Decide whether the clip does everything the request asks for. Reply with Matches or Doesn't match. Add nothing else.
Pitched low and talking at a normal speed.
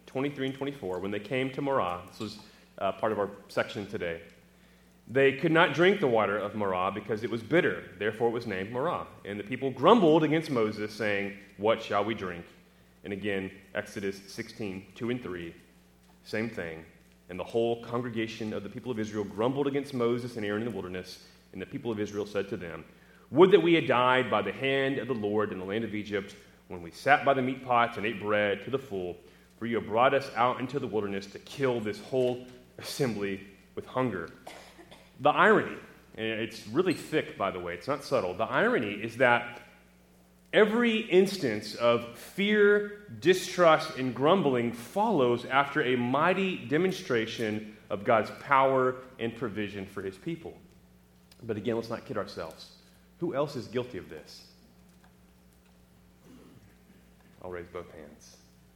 Matches